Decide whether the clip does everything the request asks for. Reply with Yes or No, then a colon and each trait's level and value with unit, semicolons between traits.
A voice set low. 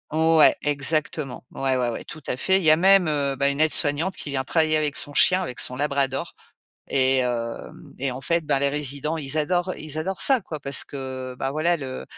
No: medium, 145 Hz